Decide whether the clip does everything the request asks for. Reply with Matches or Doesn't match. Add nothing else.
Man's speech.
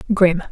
Doesn't match